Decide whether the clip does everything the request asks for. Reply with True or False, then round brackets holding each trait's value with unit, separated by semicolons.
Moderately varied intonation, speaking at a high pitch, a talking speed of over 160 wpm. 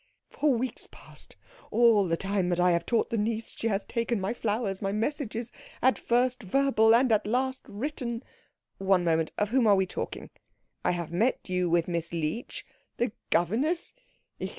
True (4.8 semitones; 215 Hz; 180 wpm)